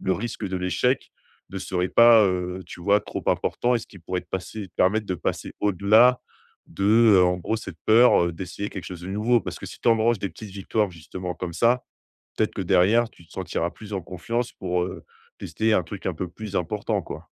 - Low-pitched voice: Yes, low, 100 Hz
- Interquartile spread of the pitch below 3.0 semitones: No, average, 3.5 semitones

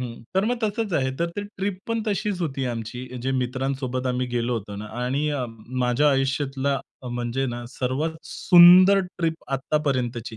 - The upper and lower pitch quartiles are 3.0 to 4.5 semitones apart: No, average, 5.3 semitones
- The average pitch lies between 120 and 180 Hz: Yes, low, 135 Hz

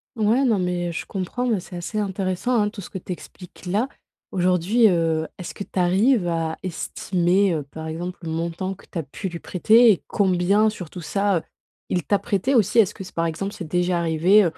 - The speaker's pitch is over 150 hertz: Yes, medium, 185 Hz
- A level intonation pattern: No, average, 3.0 semitones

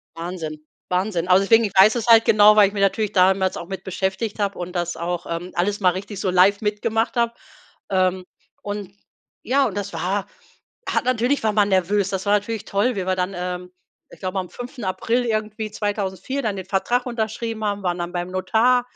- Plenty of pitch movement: No, average, 2.9 semitones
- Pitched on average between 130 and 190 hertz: No, high, 200 Hz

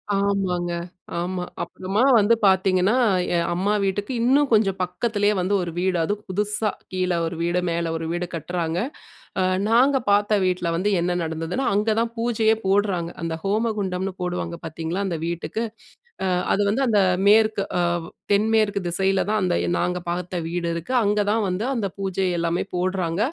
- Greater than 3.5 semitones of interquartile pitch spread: No, average, 3.1 semitones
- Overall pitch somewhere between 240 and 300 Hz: No, high, 190 Hz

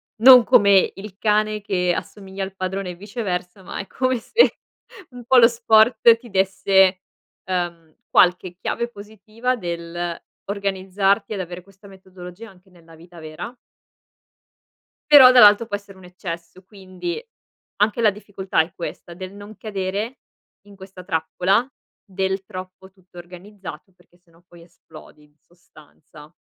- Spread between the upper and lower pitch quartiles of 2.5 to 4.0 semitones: Yes, average, 2.9 semitones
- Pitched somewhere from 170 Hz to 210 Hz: Yes, high, 190 Hz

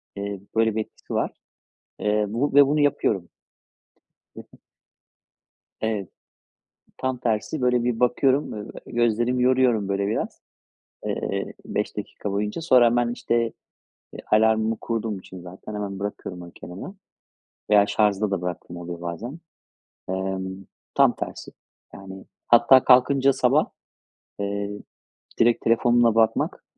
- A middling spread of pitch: Yes, average, 3.5 semitones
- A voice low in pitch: Yes, low, 110 Hz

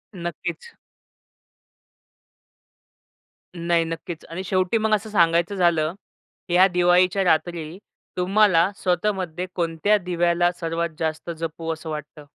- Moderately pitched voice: Yes, medium, 175 Hz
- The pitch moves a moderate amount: No, narrow, 2.1 semitones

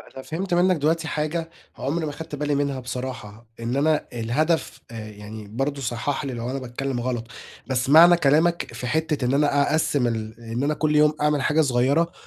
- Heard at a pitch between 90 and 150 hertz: Yes, medium, 140 Hz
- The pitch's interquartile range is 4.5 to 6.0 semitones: No, average, 4.1 semitones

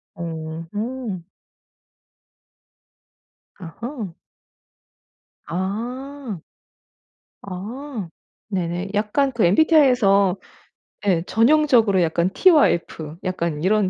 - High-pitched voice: Yes, high, 200 Hz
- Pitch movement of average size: No, wide, 6.3 semitones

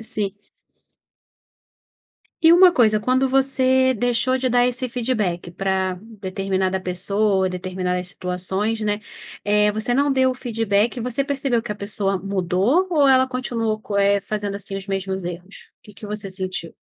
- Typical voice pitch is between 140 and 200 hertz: No, high, 210 Hz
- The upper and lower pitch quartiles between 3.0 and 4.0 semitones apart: No, average, 4.8 semitones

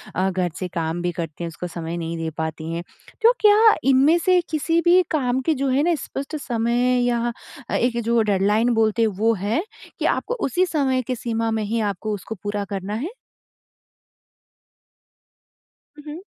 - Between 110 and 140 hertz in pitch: No, high, 230 Hz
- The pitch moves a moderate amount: No, wide, 6.3 semitones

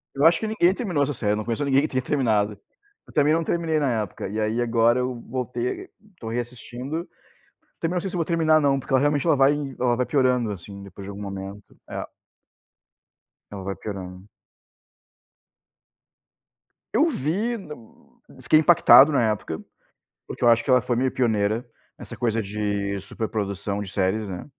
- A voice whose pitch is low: Yes, low, 120 Hz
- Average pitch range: No, wide, 5.9 semitones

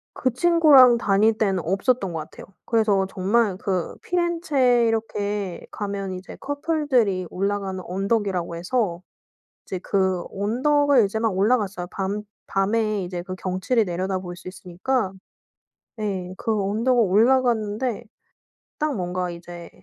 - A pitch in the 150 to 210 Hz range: Yes, high, 205 Hz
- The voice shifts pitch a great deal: No, average, 4.4 semitones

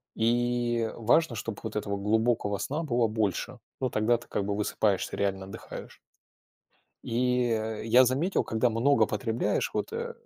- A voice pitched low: Yes, low, 115 Hz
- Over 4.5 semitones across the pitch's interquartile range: No, narrow, 2.5 semitones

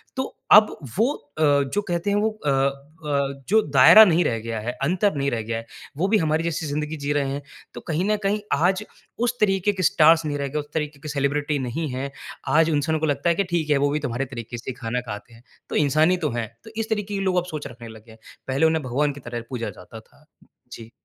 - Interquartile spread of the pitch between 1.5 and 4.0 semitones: No, average, 4.5 semitones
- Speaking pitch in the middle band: Yes, medium, 145 Hz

